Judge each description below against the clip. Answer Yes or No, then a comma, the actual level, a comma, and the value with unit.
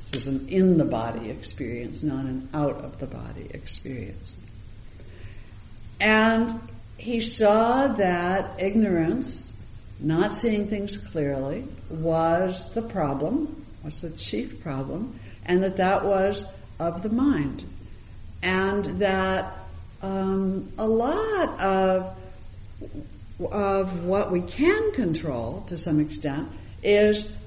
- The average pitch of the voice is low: No, medium, 175 Hz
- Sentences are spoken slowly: Yes, slow, 110 wpm